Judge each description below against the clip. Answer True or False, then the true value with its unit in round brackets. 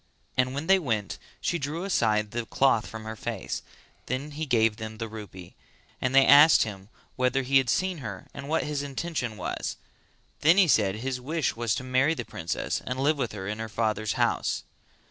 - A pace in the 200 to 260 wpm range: True (205 wpm)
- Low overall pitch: True (125 Hz)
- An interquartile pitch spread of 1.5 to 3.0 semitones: False (4.6 semitones)